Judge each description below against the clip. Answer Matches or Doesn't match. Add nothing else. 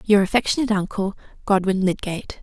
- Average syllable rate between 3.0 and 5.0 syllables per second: Doesn't match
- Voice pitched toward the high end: Matches